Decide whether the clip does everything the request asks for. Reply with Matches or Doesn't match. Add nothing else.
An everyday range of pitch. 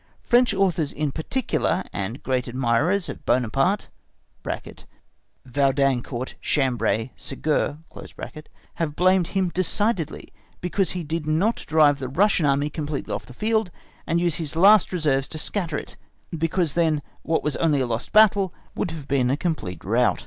Matches